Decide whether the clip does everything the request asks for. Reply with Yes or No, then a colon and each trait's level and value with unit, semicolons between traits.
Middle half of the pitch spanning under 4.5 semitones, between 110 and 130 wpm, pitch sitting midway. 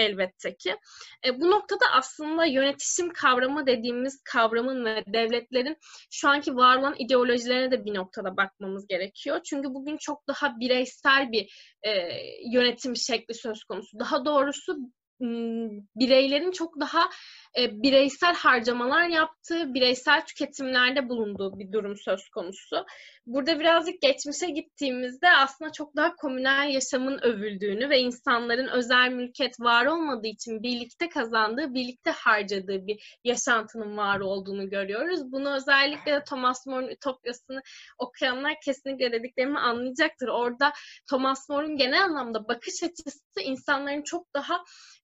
No: average, 3.6 semitones; average, 125 wpm; very high, 265 Hz